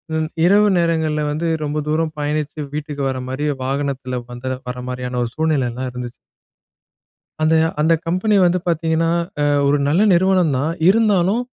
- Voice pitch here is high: No, medium, 155 Hz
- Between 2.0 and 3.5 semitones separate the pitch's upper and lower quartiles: No, average, 4.2 semitones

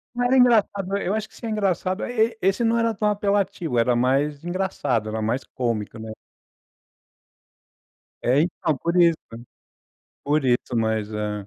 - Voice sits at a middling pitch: Yes, medium, 165 Hz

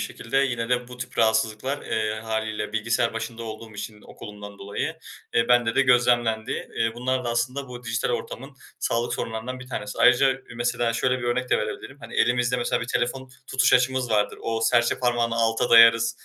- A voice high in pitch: No, low, 120 Hz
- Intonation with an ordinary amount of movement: No, narrow, 1.8 semitones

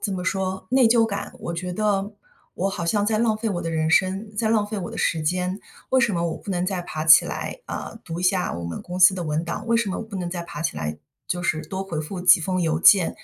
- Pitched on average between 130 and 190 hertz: Yes, medium, 185 Hz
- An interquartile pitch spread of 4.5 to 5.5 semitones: No, average, 3.4 semitones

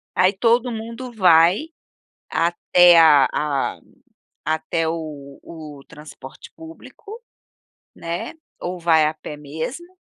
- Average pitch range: No, wide, 6.4 semitones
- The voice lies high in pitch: No, medium, 165 Hz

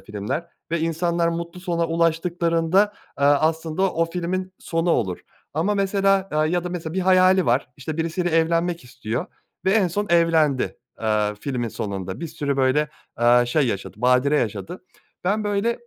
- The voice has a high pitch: No, medium, 165 Hz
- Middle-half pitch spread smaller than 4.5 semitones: No, average, 5.1 semitones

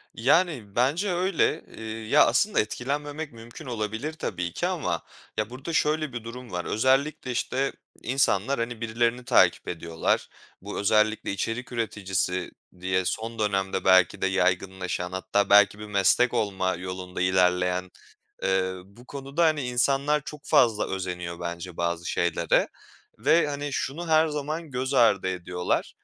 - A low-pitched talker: Yes, low, 110 Hz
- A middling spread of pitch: No, wide, 6.6 semitones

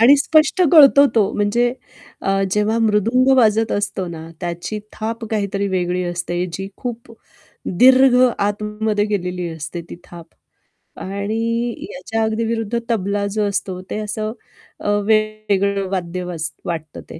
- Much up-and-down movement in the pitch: No, average, 3.5 semitones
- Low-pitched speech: No, high, 210 Hz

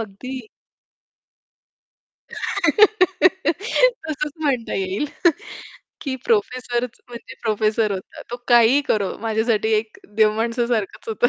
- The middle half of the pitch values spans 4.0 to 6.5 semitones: Yes, average, 5.3 semitones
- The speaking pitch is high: Yes, high, 240 Hz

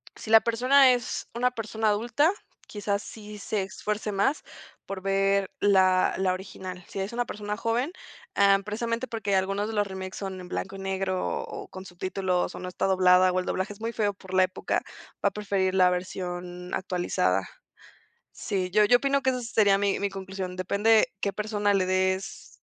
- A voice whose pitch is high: Yes, high, 195 Hz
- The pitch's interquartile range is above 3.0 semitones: No, narrow, 2.4 semitones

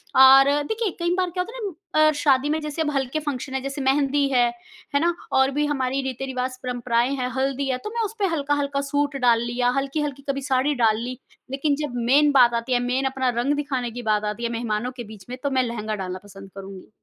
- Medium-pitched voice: No, very high, 270 Hz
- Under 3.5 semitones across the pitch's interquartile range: Yes, average, 2.9 semitones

